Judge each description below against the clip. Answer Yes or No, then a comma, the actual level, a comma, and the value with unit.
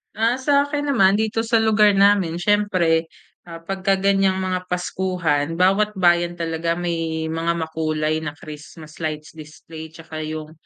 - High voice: No, medium, 175 Hz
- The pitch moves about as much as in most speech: Yes, average, 3.6 semitones